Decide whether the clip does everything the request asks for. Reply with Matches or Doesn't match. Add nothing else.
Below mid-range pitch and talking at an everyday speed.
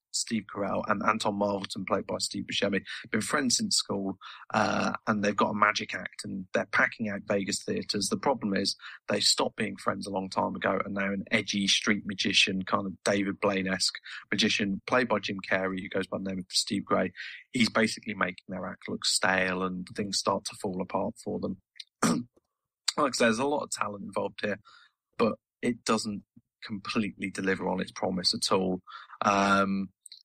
Matches